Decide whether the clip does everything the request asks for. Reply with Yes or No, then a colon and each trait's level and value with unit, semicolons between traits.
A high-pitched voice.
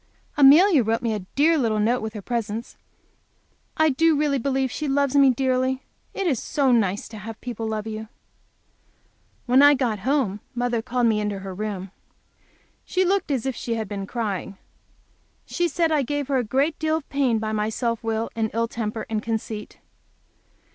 Yes: high, 240 Hz